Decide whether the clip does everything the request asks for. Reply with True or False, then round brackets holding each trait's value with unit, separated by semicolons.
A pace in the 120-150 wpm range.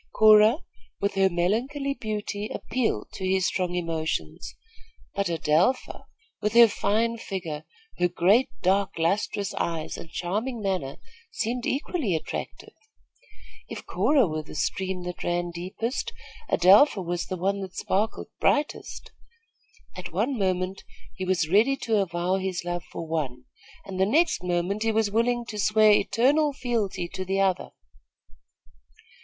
True (140 wpm)